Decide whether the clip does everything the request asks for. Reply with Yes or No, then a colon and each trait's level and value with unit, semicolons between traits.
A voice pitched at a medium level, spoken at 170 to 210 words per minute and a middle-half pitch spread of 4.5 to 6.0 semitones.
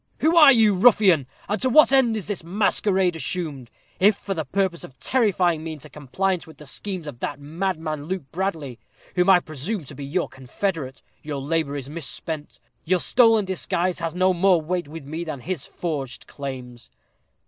Yes: medium, 170 Hz; average, 180 wpm; average, 4.9 semitones